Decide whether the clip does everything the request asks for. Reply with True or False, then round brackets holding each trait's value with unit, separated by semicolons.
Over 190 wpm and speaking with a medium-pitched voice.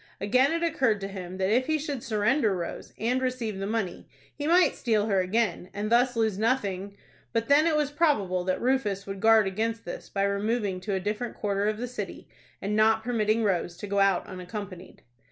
False (205 wpm; 215 Hz)